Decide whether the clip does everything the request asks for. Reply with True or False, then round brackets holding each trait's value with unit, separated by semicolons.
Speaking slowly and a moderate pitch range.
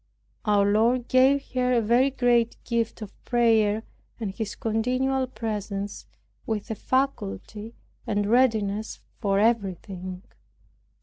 True (115 wpm; 3.1 semitones)